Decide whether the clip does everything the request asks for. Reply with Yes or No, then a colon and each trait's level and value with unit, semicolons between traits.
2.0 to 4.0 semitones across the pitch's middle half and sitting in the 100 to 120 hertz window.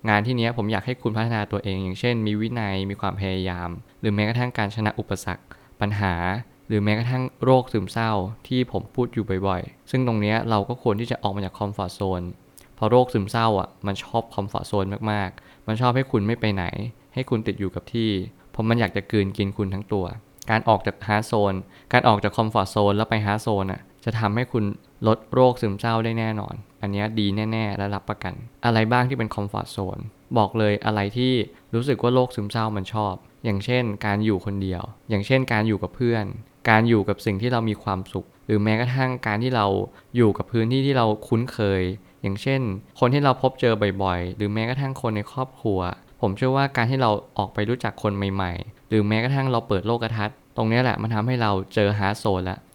Yes: average, 2.9 semitones; low, 110 Hz